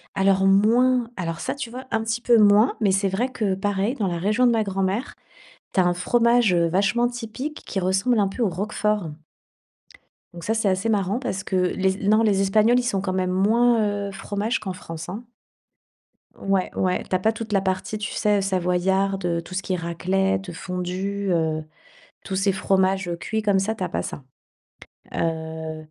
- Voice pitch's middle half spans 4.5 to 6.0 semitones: No, average, 2.9 semitones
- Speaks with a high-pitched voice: Yes, high, 195 Hz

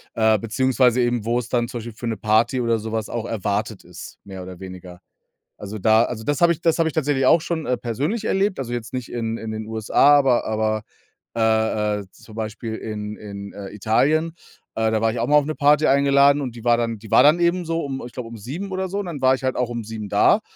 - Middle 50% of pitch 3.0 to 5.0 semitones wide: Yes, average, 4.3 semitones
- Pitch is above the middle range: No, low, 120 Hz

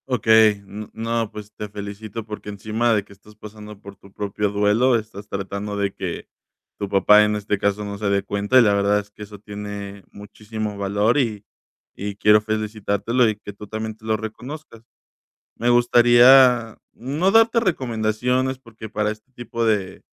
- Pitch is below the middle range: Yes, low, 105 Hz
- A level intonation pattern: Yes, narrow, 2.1 semitones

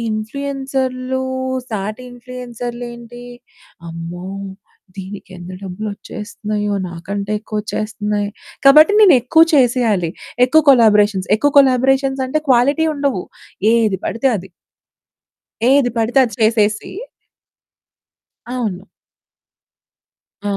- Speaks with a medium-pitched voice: No, high, 235 Hz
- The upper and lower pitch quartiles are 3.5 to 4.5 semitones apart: Yes, average, 4.1 semitones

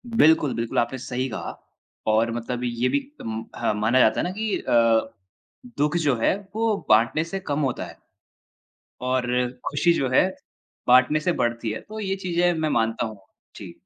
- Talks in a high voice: No, low, 130 Hz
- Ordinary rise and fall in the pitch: No, wide, 6.1 semitones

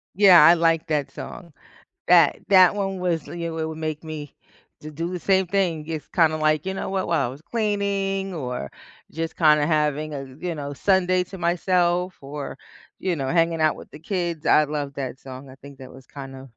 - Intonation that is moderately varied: Yes, average, 3.6 semitones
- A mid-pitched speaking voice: Yes, medium, 160 Hz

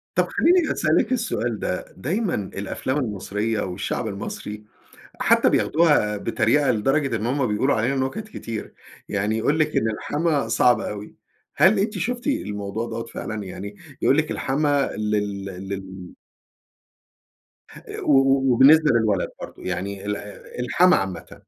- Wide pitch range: Yes, wide, 6.1 semitones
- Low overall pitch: Yes, low, 115 Hz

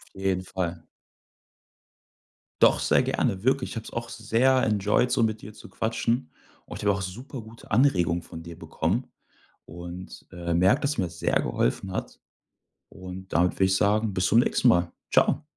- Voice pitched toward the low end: Yes, very low, 95 Hz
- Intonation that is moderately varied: Yes, average, 4.3 semitones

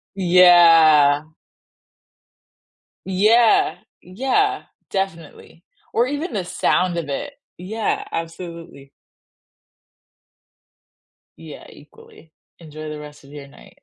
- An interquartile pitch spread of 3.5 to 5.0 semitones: Yes, average, 4.7 semitones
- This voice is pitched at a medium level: Yes, medium, 170 Hz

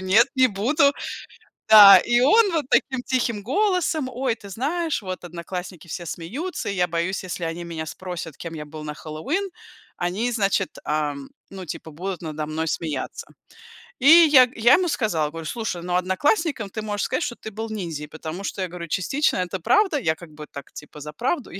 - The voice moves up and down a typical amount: No, wide, 7.5 semitones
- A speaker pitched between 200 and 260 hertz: No, high, 190 Hz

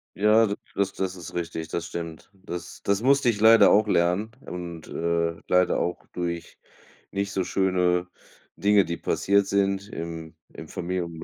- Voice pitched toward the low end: Yes, very low, 90 Hz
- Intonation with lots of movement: No, average, 2.8 semitones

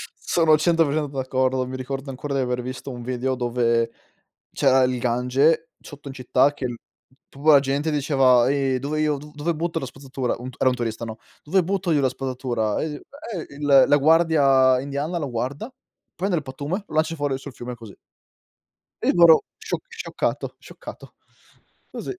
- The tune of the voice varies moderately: Yes, average, 3.2 semitones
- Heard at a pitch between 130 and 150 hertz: Yes, low, 135 Hz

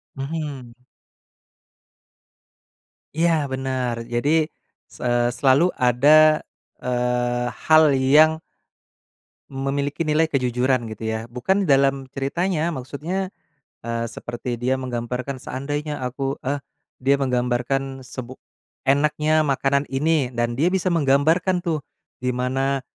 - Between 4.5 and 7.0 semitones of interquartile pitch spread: No, average, 3.4 semitones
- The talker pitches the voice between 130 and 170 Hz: Yes, low, 135 Hz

